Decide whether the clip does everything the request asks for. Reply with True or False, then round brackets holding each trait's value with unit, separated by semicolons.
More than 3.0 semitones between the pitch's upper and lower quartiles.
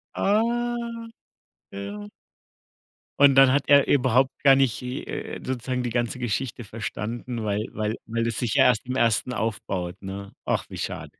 True (3.4 semitones)